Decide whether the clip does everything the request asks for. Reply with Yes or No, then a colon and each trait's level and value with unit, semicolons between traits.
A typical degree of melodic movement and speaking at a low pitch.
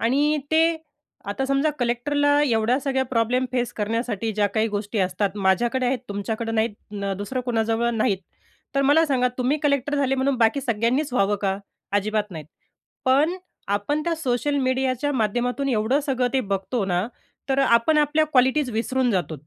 No: average, 4.1 semitones; high, 245 Hz